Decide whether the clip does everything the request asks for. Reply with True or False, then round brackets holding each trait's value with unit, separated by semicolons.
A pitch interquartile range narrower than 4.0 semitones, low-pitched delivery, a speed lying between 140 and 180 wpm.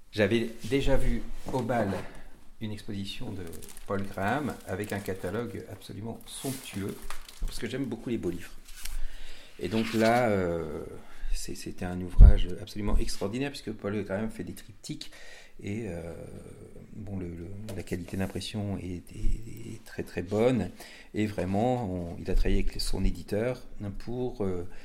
True (3.3 semitones; 100 Hz; 150 wpm)